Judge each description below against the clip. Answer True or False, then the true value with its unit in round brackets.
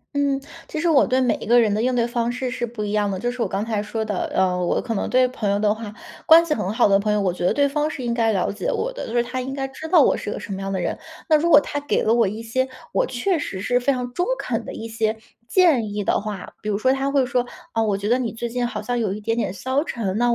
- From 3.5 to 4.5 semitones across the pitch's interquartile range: True (3.9 semitones)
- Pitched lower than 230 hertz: False (235 Hz)